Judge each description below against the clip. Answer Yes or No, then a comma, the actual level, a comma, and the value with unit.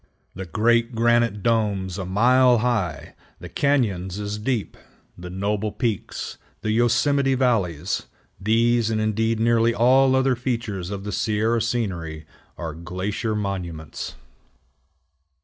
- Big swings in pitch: No, average, 3.7 semitones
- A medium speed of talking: No, slow, 120 wpm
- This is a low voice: Yes, low, 110 Hz